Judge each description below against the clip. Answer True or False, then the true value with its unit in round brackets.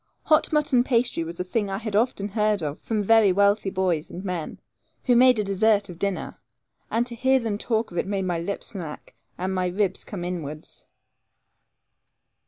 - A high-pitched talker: True (200 Hz)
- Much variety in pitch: False (3.8 semitones)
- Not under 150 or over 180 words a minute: False (190 wpm)